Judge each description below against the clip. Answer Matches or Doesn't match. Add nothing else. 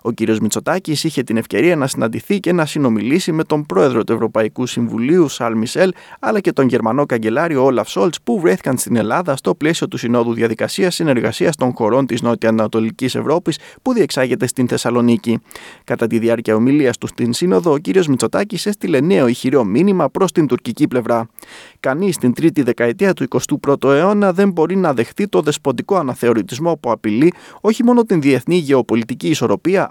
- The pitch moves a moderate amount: Doesn't match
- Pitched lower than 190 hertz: Matches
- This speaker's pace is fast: Matches